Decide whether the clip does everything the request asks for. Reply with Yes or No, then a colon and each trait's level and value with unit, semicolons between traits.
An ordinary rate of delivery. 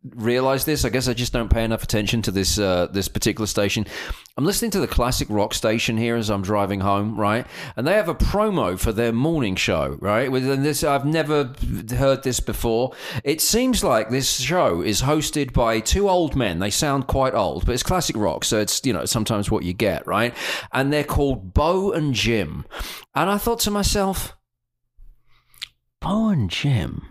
Yes: average, 195 wpm